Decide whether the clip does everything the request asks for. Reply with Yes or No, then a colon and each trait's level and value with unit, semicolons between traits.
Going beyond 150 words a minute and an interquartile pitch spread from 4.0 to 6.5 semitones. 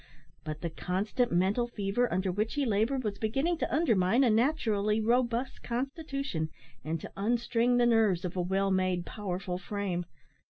Yes: average, 160 wpm; average, 4.6 semitones